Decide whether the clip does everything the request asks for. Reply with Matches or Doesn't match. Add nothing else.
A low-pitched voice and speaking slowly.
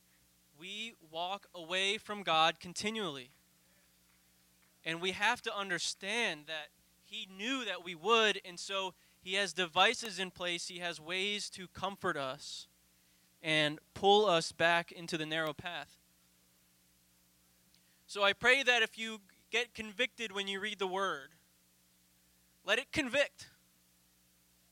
Doesn't match